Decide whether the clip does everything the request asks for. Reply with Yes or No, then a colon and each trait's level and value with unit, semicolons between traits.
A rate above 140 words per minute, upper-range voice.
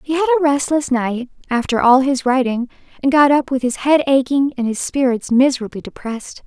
Yes: average, 195 wpm; very high, 265 Hz